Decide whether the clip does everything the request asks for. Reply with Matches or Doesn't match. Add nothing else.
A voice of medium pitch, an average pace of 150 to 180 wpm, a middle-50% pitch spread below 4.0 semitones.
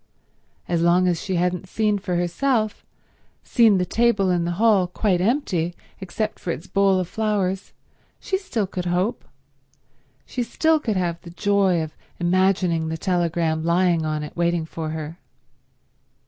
Matches